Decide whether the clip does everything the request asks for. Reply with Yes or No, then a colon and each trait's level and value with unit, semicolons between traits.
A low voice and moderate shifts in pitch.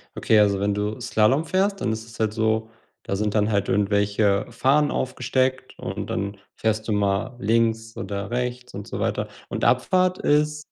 Yes: low, 110 Hz; average, 3.9 semitones